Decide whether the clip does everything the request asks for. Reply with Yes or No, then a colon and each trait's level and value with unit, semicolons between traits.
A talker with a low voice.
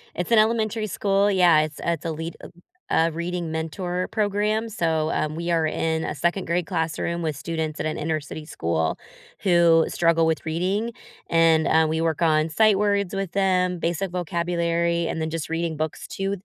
No: medium, 170 Hz